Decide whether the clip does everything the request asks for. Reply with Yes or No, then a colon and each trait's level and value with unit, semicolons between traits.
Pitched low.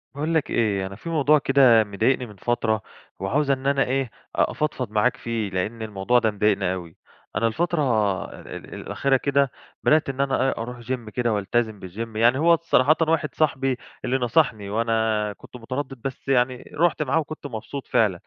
Yes: low, 125 Hz